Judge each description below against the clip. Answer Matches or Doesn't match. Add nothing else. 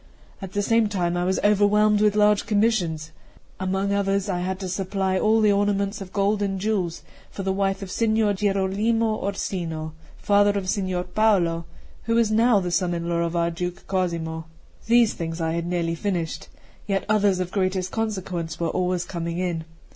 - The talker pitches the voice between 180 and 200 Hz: Matches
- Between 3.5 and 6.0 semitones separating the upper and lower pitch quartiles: Doesn't match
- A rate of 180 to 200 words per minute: Matches